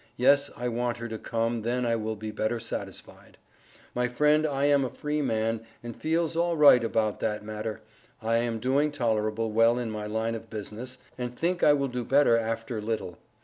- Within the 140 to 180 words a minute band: No, average, 190 wpm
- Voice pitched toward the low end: Yes, low, 115 Hz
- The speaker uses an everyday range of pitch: Yes, average, 3.5 semitones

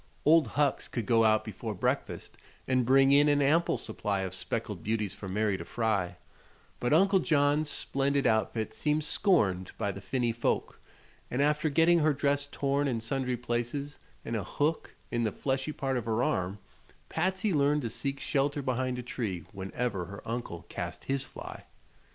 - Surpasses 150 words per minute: Yes, average, 175 wpm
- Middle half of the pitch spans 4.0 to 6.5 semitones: Yes, average, 4.9 semitones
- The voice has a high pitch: No, low, 125 Hz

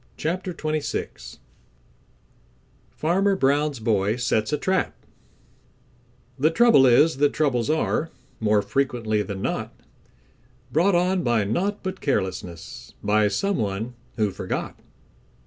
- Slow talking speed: Yes, slow, 115 wpm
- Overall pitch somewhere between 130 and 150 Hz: Yes, low, 135 Hz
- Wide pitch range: Yes, wide, 7.4 semitones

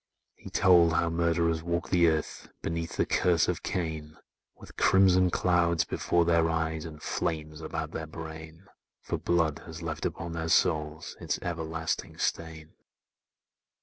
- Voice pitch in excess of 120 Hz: No, very low, 80 Hz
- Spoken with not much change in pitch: Yes, narrow, 1.2 semitones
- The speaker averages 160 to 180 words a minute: No, average, 145 wpm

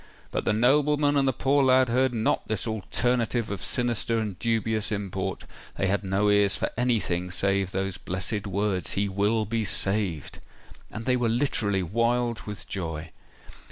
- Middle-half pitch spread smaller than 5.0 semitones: Yes, average, 3.7 semitones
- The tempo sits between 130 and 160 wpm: Yes, average, 155 wpm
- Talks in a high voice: No, low, 110 Hz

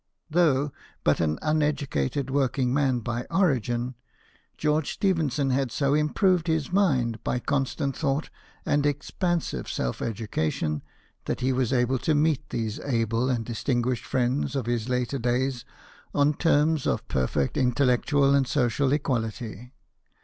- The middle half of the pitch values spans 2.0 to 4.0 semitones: Yes, average, 3.4 semitones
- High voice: No, low, 130 Hz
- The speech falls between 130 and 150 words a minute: Yes, slow, 135 wpm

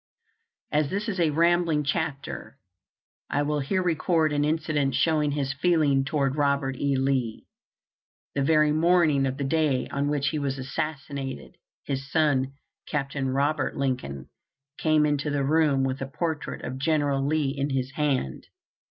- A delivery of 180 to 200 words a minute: No, average, 150 wpm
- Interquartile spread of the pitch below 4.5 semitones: Yes, narrow, 2.4 semitones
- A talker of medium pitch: Yes, medium, 145 Hz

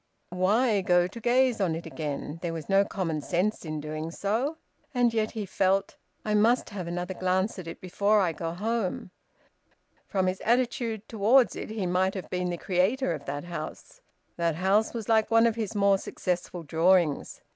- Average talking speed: Yes, average, 185 wpm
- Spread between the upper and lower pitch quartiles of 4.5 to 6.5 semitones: No, average, 4.0 semitones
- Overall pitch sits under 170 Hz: No, high, 190 Hz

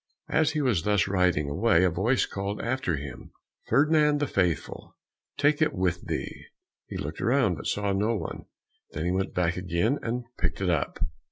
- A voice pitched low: Yes, very low, 95 Hz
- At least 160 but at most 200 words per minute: Yes, average, 180 wpm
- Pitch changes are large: Yes, wide, 6.2 semitones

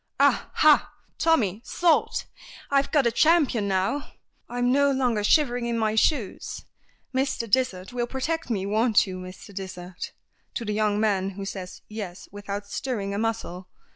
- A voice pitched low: No, high, 220 Hz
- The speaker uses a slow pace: No, average, 155 wpm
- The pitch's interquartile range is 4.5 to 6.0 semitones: Yes, average, 4.8 semitones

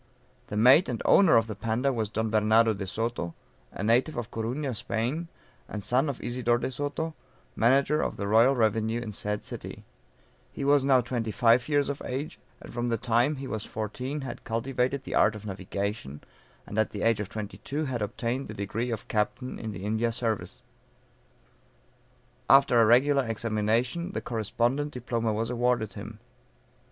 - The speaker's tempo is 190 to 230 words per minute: No, average, 175 wpm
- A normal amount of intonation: Yes, average, 3.2 semitones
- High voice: No, low, 115 Hz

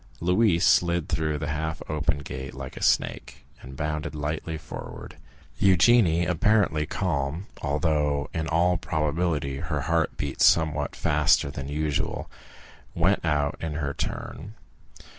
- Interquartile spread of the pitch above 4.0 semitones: No, narrow, 2.6 semitones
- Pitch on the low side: Yes, very low, 75 Hz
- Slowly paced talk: Yes, slow, 130 wpm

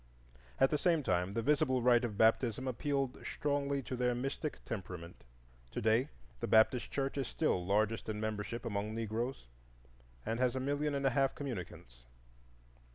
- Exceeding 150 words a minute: Yes, average, 160 wpm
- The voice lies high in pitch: No, low, 120 Hz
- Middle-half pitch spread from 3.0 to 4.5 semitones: Yes, average, 4.0 semitones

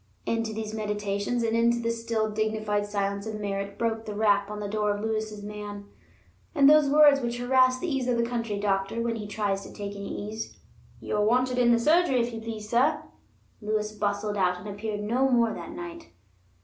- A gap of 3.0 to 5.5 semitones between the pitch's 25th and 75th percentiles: No, narrow, 2.4 semitones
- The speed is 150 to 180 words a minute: No, average, 200 wpm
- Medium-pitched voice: No, high, 215 Hz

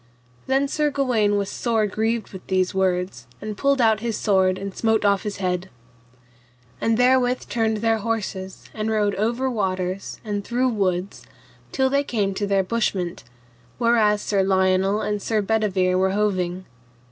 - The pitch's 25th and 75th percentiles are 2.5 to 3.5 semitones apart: Yes, average, 3.2 semitones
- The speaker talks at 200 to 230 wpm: No, average, 160 wpm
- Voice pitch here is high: Yes, high, 210 Hz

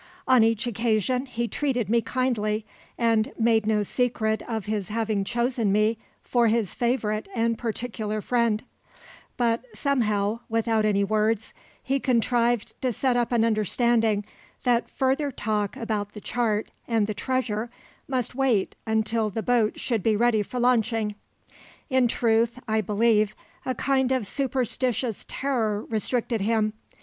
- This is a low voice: No, high, 225 Hz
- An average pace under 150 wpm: Yes, average, 140 wpm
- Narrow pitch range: Yes, narrow, 2.3 semitones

